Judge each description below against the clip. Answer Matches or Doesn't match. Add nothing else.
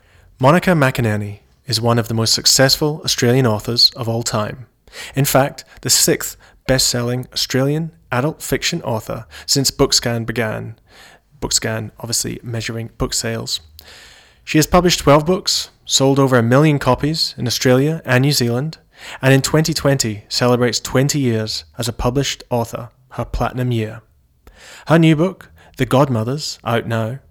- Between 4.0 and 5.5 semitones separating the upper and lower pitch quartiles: Doesn't match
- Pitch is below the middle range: Matches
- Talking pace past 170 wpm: Doesn't match